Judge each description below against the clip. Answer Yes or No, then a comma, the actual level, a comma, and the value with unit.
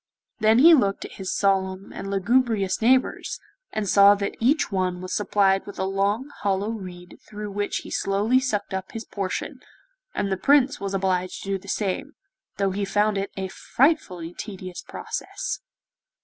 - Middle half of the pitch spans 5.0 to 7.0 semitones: No, narrow, 2.4 semitones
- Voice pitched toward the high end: Yes, high, 200 Hz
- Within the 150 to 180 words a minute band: Yes, average, 170 wpm